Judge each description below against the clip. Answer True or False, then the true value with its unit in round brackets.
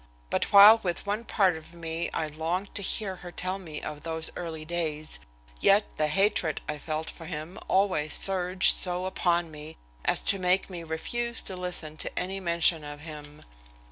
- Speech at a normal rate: True (180 wpm)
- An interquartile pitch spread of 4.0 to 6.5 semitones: False (3.2 semitones)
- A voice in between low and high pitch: True (170 Hz)